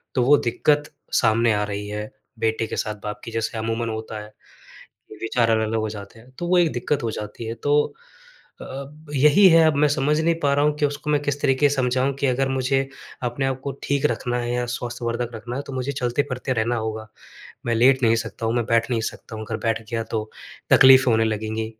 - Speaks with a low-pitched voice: Yes, low, 120 Hz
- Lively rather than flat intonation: No, average, 3.7 semitones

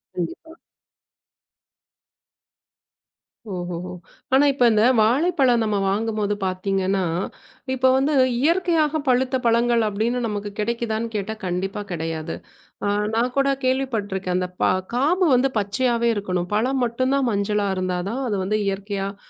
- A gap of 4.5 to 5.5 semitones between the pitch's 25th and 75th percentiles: Yes, average, 4.8 semitones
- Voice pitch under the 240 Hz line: Yes, high, 220 Hz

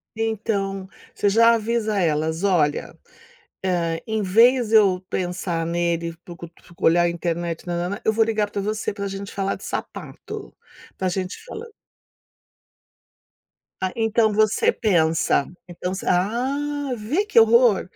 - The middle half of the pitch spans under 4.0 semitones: No, average, 4.4 semitones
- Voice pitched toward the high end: Yes, high, 200 Hz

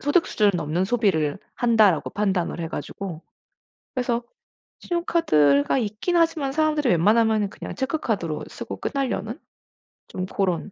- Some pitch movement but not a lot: No, wide, 7.4 semitones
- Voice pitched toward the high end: Yes, high, 215 Hz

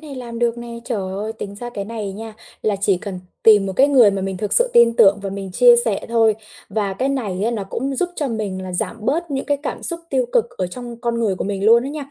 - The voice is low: No, high, 225 Hz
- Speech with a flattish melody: No, average, 3.8 semitones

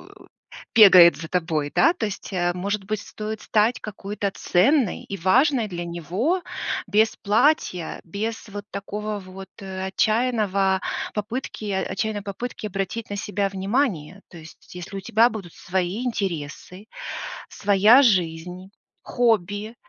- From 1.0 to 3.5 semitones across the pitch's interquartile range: Yes, average, 2.9 semitones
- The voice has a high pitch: Yes, high, 200 Hz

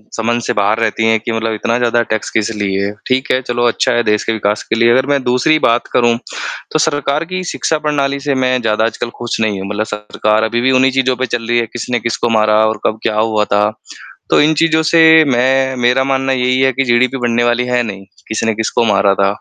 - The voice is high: No, low, 120 Hz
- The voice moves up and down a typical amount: Yes, average, 3.1 semitones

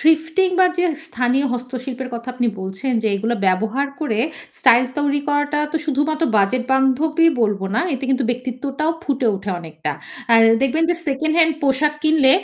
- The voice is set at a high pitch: Yes, very high, 265 Hz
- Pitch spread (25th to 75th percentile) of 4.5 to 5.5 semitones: No, average, 3.9 semitones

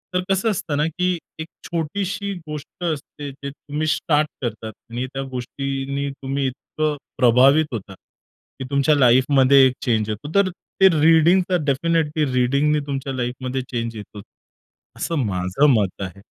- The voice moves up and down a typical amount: Yes, average, 3.8 semitones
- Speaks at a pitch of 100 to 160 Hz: Yes, medium, 140 Hz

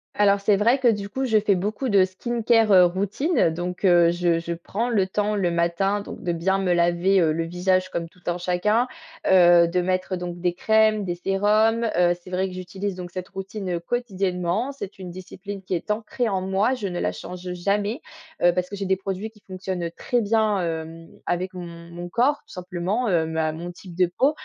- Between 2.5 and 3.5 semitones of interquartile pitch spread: Yes, average, 2.9 semitones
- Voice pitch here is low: No, medium, 185 Hz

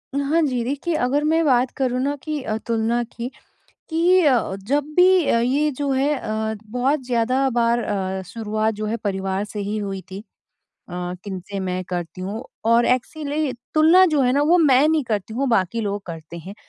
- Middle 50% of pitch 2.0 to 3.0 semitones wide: No, average, 5.3 semitones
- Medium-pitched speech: No, high, 245 Hz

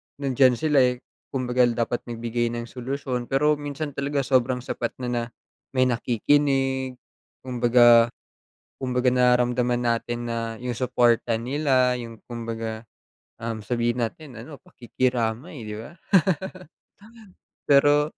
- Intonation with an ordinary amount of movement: No, narrow, 2.1 semitones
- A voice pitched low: Yes, low, 125 Hz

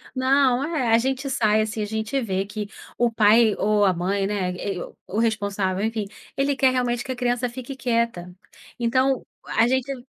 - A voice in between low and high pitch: No, high, 230 Hz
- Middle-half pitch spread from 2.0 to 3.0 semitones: No, average, 3.7 semitones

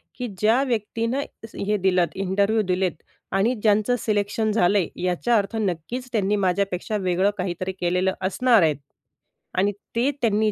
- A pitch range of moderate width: Yes, average, 3.3 semitones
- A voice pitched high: Yes, high, 205 Hz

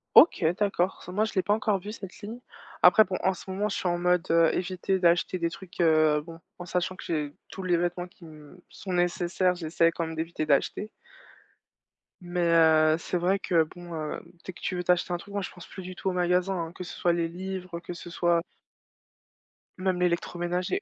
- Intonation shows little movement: Yes, narrow, 1.8 semitones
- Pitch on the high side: No, medium, 175 Hz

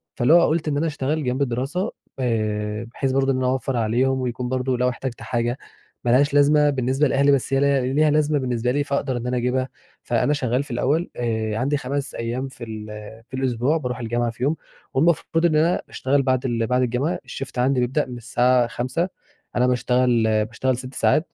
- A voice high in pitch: No, low, 130 Hz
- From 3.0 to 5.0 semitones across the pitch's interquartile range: No, narrow, 2.6 semitones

